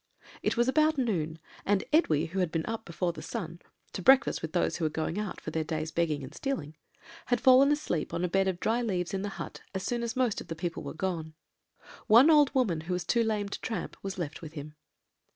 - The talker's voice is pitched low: No, medium, 185 Hz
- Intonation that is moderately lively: No, wide, 6.4 semitones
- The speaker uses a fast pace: Yes, fast, 240 wpm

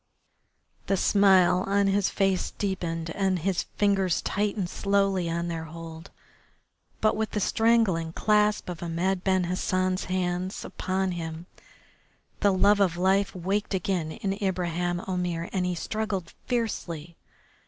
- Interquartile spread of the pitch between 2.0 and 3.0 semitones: Yes, narrow, 2.4 semitones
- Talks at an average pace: No, slow, 130 wpm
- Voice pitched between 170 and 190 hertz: Yes, medium, 185 Hz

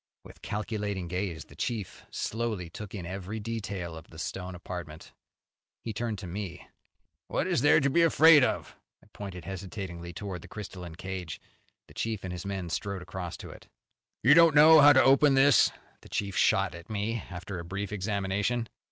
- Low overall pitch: Yes, low, 100 Hz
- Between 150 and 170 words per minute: No, average, 185 wpm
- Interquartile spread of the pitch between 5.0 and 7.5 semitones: No, average, 4.1 semitones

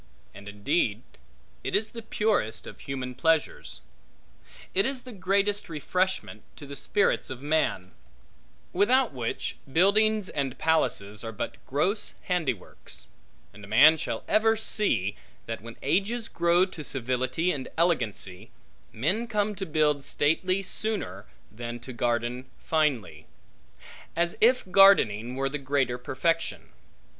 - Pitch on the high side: No, medium, 150 Hz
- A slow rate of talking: Yes, slow, 130 wpm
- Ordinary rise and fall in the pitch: No, wide, 8.1 semitones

